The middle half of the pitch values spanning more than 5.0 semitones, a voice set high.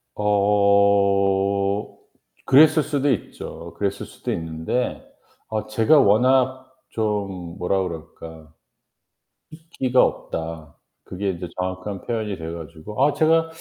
No: wide, 5.5 semitones; low, 100 Hz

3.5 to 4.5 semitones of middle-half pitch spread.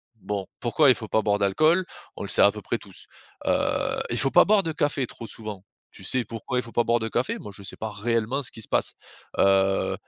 Yes: average, 3.9 semitones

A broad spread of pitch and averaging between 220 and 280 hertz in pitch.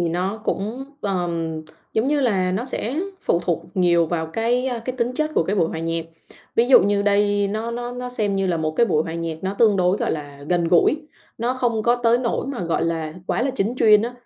No: wide, 5.9 semitones; high, 205 Hz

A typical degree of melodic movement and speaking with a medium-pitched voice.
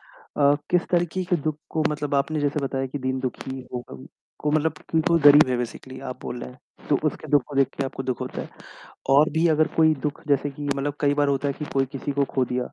No: narrow, 2.3 semitones; medium, 145 Hz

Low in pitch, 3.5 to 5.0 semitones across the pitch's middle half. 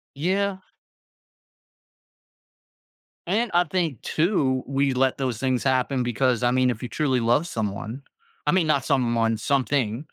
Yes: low, 130 Hz; average, 3.8 semitones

